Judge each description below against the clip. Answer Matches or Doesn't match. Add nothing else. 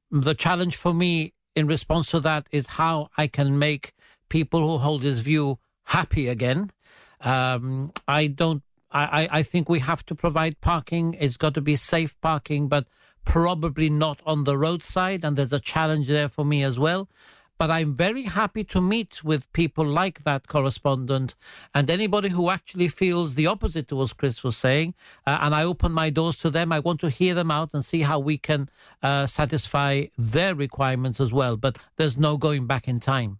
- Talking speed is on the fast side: Doesn't match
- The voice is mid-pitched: Matches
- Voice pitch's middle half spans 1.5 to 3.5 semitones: Matches